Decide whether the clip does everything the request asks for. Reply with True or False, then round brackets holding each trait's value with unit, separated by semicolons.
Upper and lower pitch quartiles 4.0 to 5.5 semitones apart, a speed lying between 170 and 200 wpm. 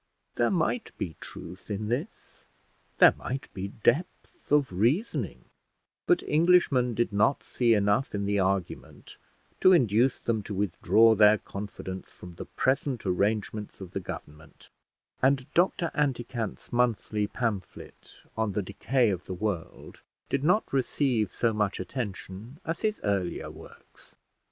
False (5.1 semitones; 135 wpm)